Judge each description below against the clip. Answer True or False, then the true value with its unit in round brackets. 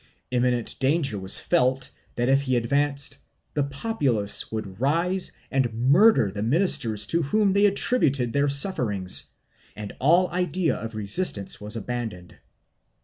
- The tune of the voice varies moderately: False (6.8 semitones)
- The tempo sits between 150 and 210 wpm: False (140 wpm)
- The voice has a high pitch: False (135 Hz)